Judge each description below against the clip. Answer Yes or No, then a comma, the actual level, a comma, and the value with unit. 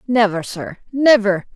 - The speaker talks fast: No, slow, 115 wpm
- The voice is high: Yes, high, 220 Hz